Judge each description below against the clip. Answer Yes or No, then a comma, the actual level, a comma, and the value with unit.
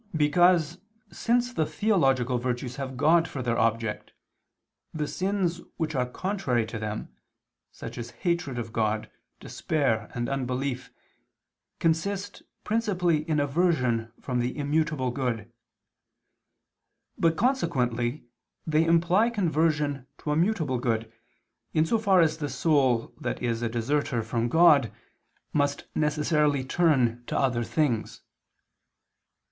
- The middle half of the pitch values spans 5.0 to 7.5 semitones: Yes, wide, 5.4 semitones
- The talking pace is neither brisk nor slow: No, slow, 120 wpm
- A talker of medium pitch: Yes, medium, 145 Hz